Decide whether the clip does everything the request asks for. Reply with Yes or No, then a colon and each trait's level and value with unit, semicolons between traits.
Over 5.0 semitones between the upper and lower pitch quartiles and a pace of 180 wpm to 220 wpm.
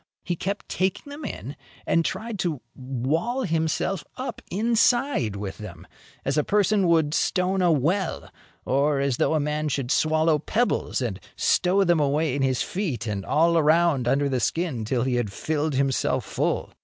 No: wide, 5.5 semitones; average, 170 wpm